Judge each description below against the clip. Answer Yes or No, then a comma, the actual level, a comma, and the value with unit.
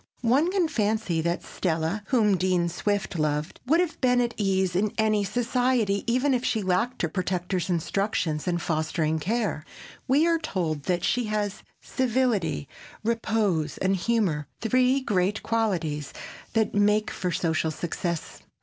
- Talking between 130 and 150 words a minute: Yes, average, 145 wpm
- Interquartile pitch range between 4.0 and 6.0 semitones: Yes, average, 5.3 semitones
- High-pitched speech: Yes, high, 200 Hz